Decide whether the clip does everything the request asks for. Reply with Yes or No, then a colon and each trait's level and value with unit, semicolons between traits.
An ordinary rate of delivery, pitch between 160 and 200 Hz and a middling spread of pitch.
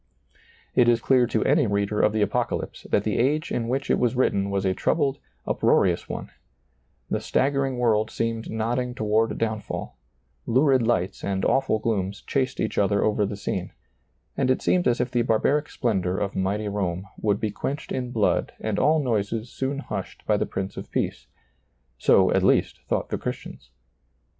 No: average, 180 wpm; low, 115 Hz; average, 4.1 semitones